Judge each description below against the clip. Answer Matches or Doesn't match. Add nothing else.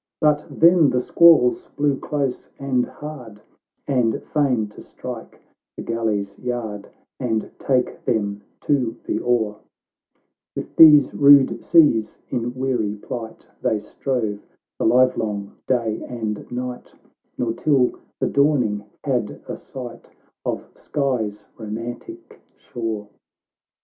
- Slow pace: Matches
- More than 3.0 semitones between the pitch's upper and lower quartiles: Matches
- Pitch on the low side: Matches